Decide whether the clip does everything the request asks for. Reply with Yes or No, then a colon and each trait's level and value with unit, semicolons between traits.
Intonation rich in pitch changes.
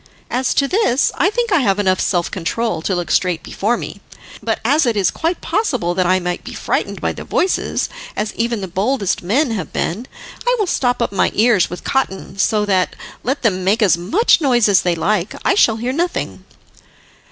Yes: wide, 6.1 semitones